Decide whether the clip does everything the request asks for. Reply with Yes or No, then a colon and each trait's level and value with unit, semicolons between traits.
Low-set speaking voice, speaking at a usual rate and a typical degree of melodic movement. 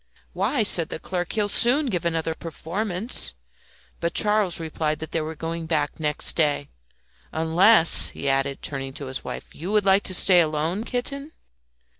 No: medium, 170 Hz; average, 170 wpm; average, 4.7 semitones